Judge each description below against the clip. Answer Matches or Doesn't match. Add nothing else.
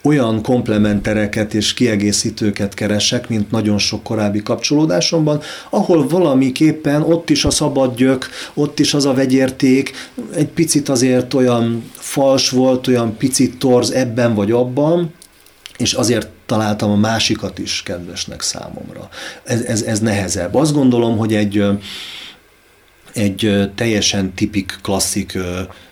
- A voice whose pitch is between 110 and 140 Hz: Matches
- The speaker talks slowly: Doesn't match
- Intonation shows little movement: Doesn't match